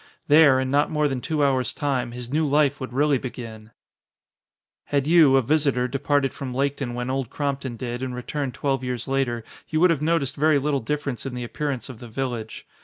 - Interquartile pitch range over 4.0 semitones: No, average, 2.7 semitones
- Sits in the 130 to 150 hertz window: Yes, low, 135 Hz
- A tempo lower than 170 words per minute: No, average, 200 wpm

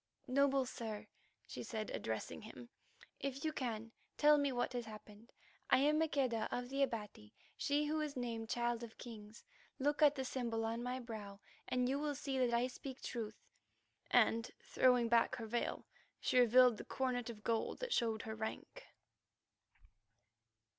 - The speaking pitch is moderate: No, high, 245 Hz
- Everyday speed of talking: Yes, average, 165 wpm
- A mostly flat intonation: No, average, 3.2 semitones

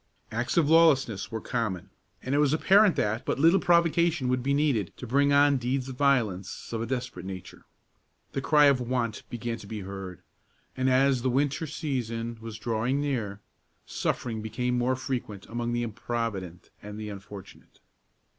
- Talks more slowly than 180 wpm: Yes, average, 170 wpm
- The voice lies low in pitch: Yes, low, 125 Hz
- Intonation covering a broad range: No, average, 4.1 semitones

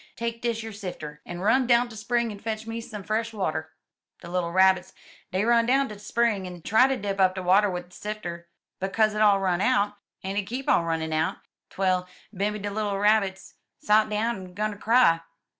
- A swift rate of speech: Yes, fast, 220 wpm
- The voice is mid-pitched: No, high, 205 Hz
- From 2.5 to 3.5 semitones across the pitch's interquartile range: Yes, average, 3.2 semitones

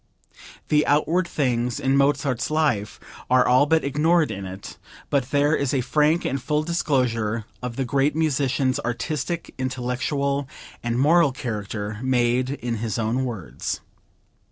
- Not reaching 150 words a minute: Yes, average, 140 wpm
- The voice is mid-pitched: No, low, 130 Hz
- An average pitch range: Yes, average, 3.6 semitones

